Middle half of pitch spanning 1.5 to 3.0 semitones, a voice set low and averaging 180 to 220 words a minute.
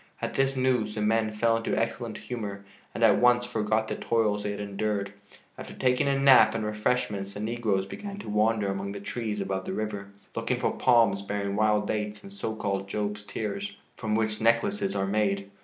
Yes: narrow, 2.4 semitones; low, 105 Hz; average, 195 wpm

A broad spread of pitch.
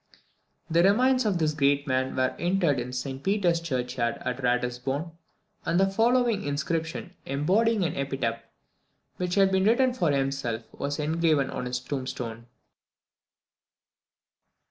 Yes: wide, 6.6 semitones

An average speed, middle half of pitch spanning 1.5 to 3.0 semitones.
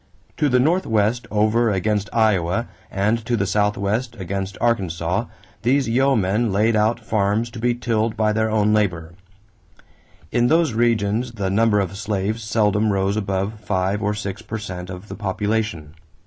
Yes: average, 155 wpm; average, 2.7 semitones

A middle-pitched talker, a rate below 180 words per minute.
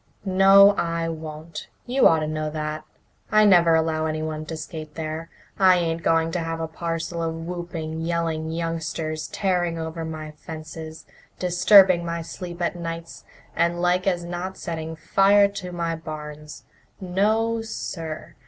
Yes: medium, 165 Hz; average, 150 wpm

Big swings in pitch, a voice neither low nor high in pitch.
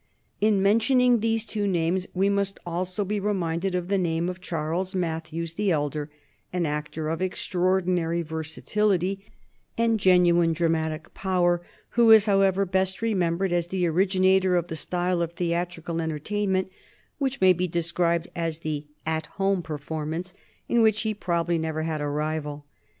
No: average, 3.0 semitones; medium, 175 Hz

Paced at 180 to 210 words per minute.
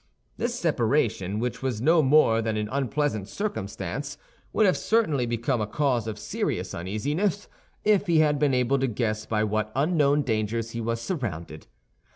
No: average, 165 wpm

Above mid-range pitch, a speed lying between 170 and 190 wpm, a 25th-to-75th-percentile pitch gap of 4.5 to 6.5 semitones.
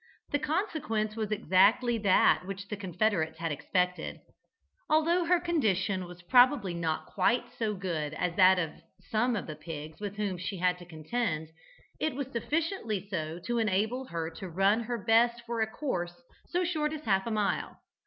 Yes: high, 205 Hz; average, 175 wpm; average, 5.2 semitones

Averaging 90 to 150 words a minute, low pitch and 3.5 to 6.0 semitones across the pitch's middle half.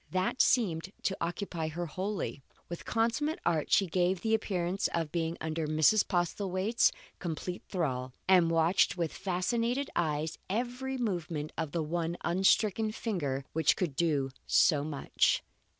No: average, 140 wpm; medium, 175 Hz; average, 4.0 semitones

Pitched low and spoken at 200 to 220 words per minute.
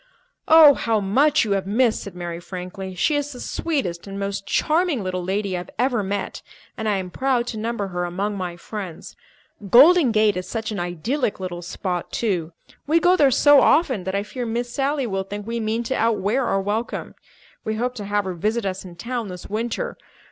No: high, 210 Hz; fast, 205 wpm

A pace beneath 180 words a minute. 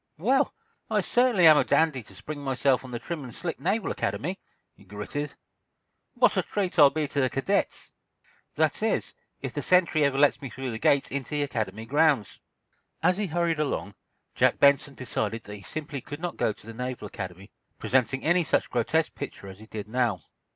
No: average, 195 wpm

